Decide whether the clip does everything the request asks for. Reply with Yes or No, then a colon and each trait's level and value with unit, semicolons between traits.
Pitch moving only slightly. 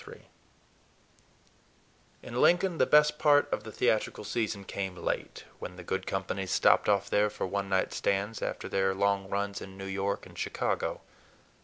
Yes: narrow, 2.3 semitones